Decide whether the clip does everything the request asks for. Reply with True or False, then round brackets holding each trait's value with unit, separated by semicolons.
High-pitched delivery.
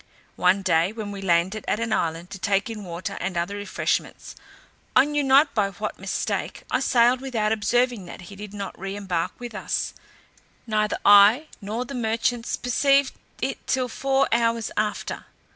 True (215 Hz)